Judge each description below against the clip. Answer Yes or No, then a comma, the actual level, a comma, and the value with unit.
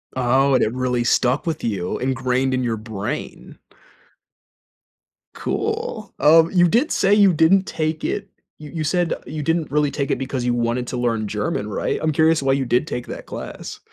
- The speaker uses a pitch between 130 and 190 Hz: Yes, low, 135 Hz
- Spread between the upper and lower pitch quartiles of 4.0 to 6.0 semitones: Yes, average, 4.6 semitones